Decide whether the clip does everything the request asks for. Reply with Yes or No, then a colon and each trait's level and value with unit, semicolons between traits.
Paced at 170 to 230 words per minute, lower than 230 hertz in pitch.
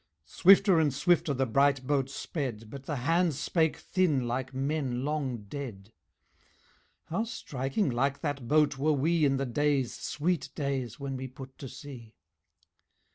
No: average, 150 wpm; medium, 140 Hz